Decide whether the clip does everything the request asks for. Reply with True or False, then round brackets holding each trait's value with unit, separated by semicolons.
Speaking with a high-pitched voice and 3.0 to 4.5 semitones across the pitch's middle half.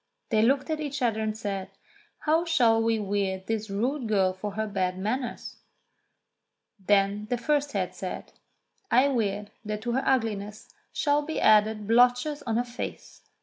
True (220 Hz; 3.8 semitones)